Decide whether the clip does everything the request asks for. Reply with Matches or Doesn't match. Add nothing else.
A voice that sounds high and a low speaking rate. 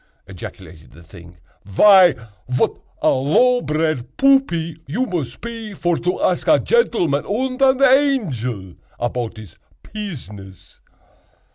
Doesn't match